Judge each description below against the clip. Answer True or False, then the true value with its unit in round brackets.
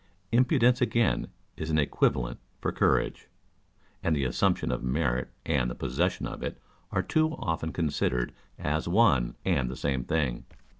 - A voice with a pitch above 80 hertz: False (75 Hz)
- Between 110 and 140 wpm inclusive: False (150 wpm)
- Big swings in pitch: True (6.4 semitones)